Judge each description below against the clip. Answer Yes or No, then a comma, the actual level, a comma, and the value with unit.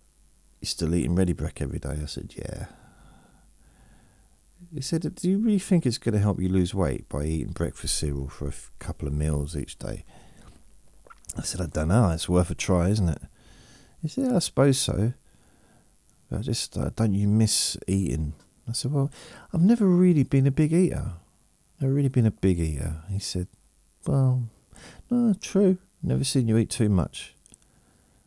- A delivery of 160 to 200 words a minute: Yes, average, 180 wpm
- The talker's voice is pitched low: Yes, very low, 95 Hz